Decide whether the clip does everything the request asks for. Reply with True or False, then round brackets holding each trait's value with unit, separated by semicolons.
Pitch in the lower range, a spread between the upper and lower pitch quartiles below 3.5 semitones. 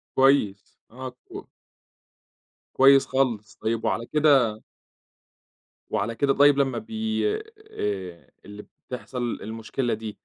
False (125 Hz; 4.1 semitones)